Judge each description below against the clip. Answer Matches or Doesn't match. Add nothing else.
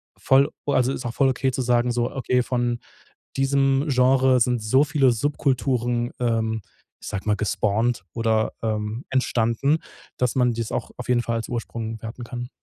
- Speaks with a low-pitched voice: Matches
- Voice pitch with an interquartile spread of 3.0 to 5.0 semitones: Doesn't match